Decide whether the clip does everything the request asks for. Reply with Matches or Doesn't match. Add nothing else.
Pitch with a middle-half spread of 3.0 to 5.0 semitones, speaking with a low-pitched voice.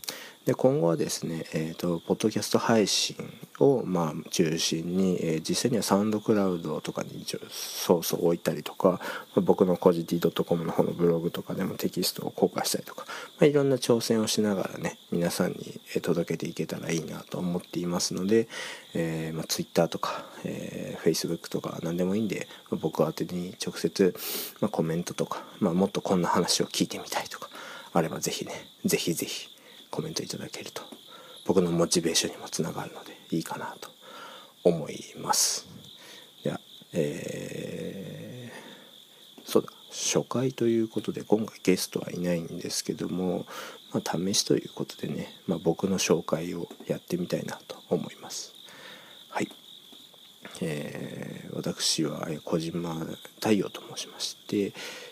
Matches